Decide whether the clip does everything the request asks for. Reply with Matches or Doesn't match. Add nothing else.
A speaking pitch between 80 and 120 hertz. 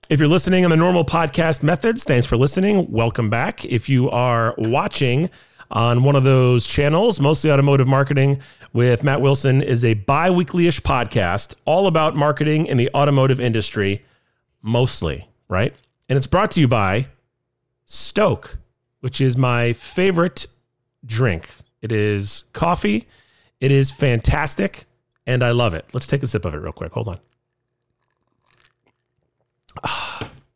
Doesn't match